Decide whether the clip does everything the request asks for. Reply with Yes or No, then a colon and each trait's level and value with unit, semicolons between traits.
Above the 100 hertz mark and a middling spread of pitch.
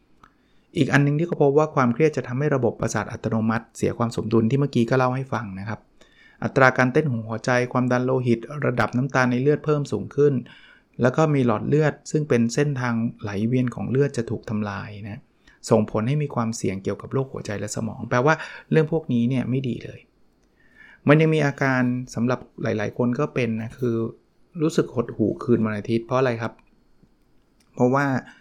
Yes: low, 125 Hz; average, 3.7 semitones